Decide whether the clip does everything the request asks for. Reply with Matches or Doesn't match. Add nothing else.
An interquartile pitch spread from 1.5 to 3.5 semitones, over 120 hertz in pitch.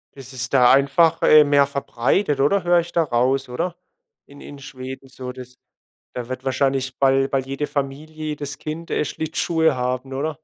Matches